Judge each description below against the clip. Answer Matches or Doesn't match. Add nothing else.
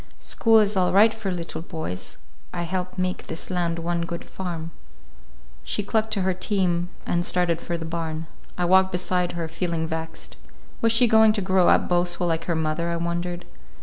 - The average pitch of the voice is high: Doesn't match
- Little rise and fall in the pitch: Matches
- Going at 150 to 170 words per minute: Doesn't match